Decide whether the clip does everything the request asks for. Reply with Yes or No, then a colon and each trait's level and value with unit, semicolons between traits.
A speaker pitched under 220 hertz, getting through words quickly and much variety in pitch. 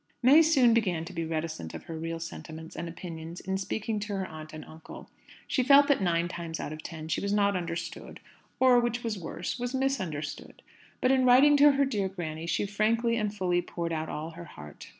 Yes: medium, 185 Hz; fast, 210 wpm; wide, 6.4 semitones